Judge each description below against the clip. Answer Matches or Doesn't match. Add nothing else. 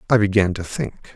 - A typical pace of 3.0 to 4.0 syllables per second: Doesn't match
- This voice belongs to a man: Matches